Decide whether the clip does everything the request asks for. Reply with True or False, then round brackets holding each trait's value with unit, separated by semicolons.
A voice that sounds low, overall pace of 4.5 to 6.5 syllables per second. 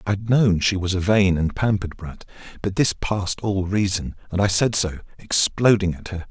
True (95 Hz; 4.9 syllables/s)